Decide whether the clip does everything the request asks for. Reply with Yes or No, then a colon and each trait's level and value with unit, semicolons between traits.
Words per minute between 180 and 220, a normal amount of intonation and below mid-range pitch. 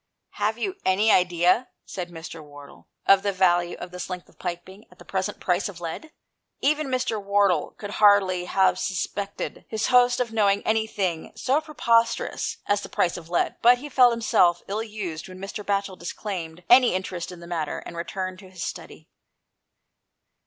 No: average, 190 wpm; average, 3.7 semitones; high, 195 Hz